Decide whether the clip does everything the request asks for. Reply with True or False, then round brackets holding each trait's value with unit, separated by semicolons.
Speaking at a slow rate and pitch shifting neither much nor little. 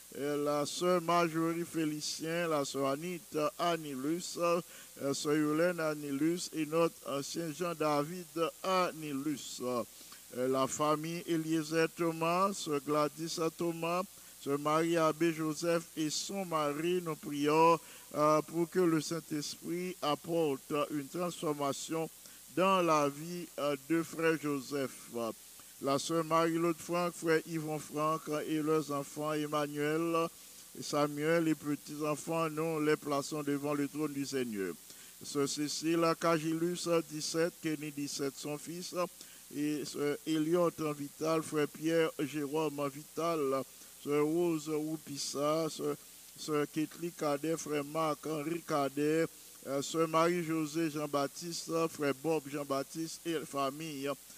False (120 wpm; 2.1 semitones)